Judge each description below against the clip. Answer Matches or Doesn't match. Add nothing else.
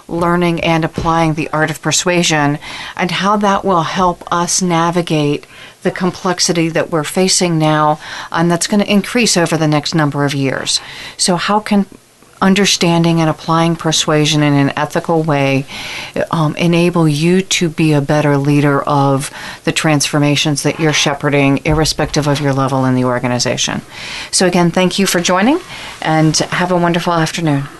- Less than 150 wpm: Doesn't match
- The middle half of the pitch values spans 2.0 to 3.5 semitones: Matches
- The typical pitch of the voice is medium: Matches